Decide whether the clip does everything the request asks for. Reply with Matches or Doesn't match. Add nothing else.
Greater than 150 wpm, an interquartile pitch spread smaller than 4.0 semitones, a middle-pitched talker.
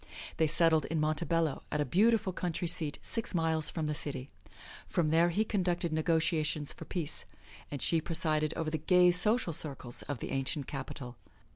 Matches